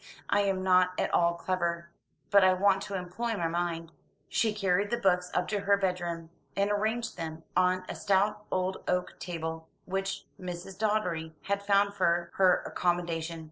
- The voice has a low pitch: No, medium, 185 Hz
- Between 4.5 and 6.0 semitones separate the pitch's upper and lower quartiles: No, average, 2.7 semitones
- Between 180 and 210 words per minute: No, average, 170 wpm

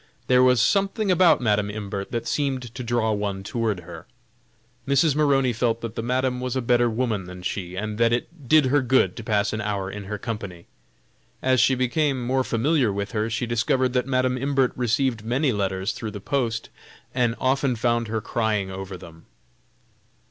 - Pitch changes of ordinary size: Yes, average, 3.6 semitones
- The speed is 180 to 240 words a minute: Yes, average, 185 wpm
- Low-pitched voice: Yes, low, 120 Hz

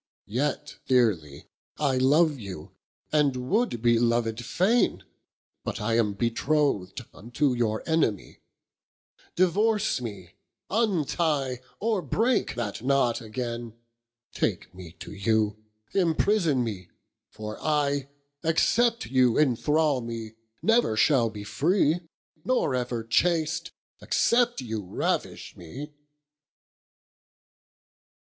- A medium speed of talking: No, slow, 100 wpm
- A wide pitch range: Yes, wide, 6.2 semitones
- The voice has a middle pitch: No, low, 130 Hz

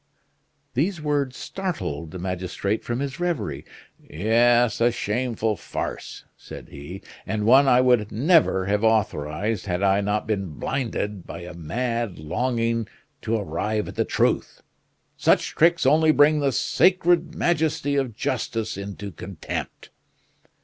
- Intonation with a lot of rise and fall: Yes, wide, 5.7 semitones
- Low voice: Yes, low, 115 Hz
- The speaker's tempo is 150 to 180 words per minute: No, slow, 135 wpm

